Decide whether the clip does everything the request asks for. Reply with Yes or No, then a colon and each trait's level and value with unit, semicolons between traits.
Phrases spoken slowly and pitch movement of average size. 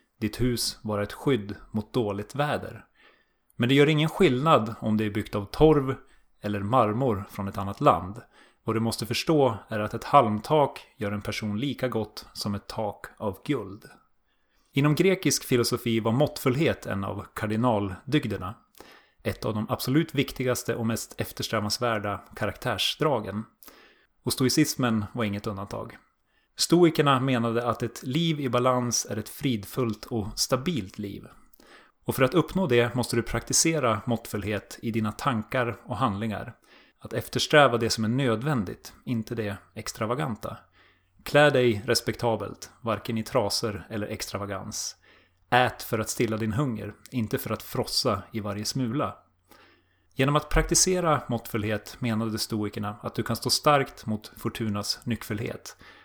No: average, 145 wpm; average, 3.6 semitones